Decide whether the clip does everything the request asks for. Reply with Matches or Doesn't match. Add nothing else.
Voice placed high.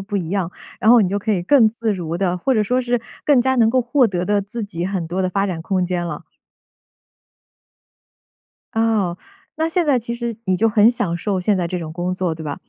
Matches